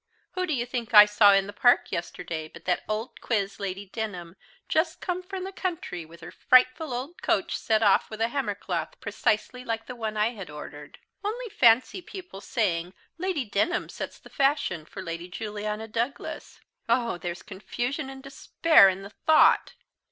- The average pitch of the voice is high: Yes, high, 225 Hz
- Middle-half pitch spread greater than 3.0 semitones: Yes, wide, 5.6 semitones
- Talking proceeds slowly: No, average, 180 wpm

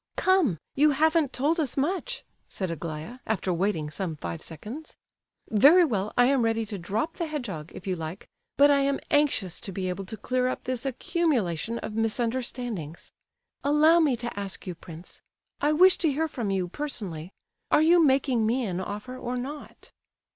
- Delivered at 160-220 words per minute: Yes, average, 170 wpm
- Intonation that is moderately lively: No, wide, 7.4 semitones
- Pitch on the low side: No, high, 240 Hz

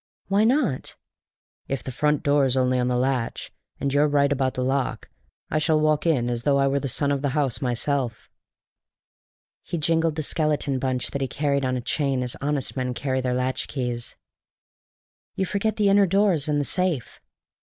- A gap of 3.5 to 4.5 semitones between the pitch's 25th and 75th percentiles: No, average, 3.0 semitones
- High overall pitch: No, medium, 140 Hz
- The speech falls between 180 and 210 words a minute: Yes, average, 190 wpm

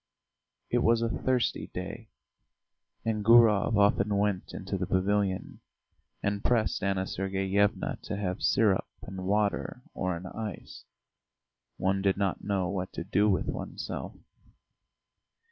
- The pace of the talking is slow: Yes, slow, 130 wpm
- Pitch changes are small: Yes, narrow, 1.8 semitones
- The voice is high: No, low, 100 Hz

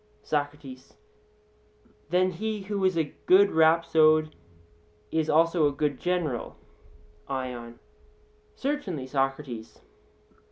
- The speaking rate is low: Yes, slow, 90 wpm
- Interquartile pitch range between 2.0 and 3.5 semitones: No, average, 4.9 semitones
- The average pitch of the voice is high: No, medium, 155 Hz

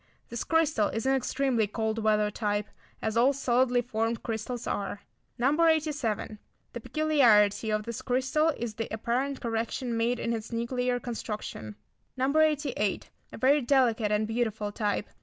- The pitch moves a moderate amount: Yes, average, 3.3 semitones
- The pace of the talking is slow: No, average, 150 wpm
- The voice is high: Yes, high, 235 Hz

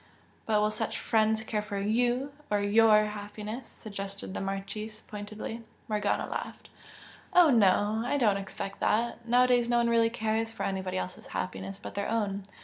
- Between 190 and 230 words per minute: No, average, 165 wpm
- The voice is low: No, high, 215 Hz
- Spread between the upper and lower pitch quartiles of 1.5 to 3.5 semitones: Yes, narrow, 2.4 semitones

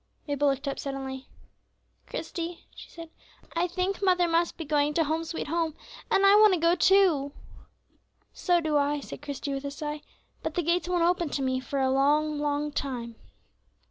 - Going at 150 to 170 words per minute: No, average, 185 wpm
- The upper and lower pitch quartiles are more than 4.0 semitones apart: No, average, 3.4 semitones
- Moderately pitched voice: No, very high, 300 Hz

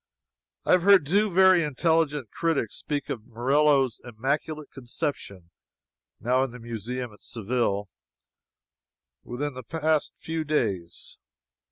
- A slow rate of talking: Yes, slow, 120 wpm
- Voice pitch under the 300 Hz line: Yes, low, 135 Hz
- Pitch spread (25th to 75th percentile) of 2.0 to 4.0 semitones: No, average, 4.9 semitones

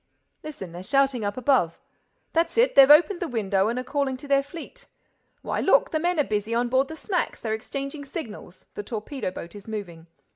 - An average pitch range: No, wide, 6.2 semitones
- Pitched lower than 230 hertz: No, very high, 260 Hz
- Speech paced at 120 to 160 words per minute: No, average, 180 wpm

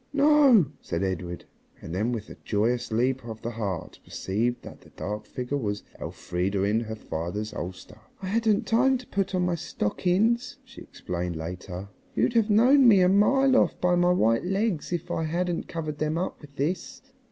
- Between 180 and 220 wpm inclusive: Yes, average, 185 wpm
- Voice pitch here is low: No, medium, 145 Hz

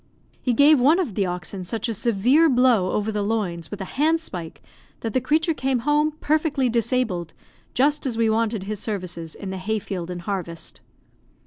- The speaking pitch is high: Yes, high, 225 Hz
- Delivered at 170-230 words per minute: Yes, average, 185 wpm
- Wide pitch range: Yes, wide, 6.1 semitones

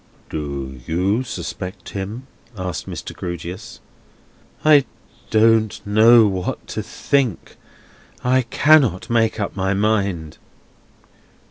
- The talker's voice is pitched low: Yes, low, 100 Hz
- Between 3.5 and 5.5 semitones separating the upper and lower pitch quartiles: Yes, average, 4.1 semitones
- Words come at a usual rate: No, slow, 100 wpm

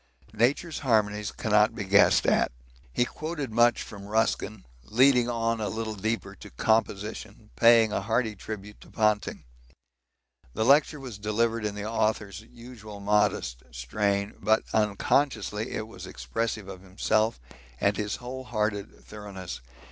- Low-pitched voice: Yes, low, 110 Hz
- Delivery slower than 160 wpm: Yes, average, 140 wpm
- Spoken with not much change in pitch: Yes, narrow, 2.0 semitones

